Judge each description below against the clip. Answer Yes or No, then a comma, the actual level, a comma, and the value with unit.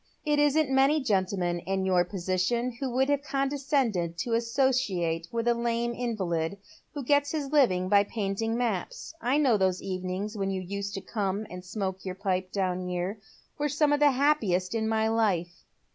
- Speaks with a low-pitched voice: No, high, 215 Hz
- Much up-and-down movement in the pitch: Yes, wide, 6.1 semitones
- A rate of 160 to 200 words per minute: Yes, average, 175 wpm